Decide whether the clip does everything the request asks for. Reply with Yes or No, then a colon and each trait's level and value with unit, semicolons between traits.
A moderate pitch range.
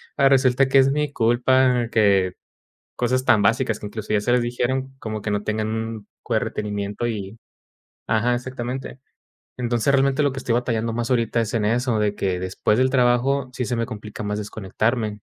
Yes: average, 3.1 semitones